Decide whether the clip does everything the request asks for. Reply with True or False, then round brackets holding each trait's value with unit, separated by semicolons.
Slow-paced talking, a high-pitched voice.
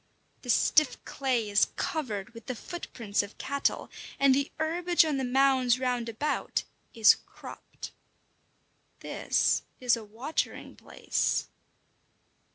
True (125 wpm; 255 Hz)